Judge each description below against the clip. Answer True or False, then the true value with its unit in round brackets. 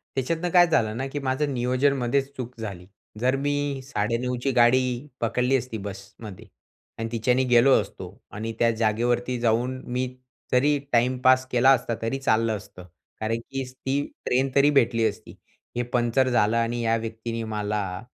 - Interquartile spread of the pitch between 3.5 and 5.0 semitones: False (2.6 semitones)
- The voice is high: False (120 Hz)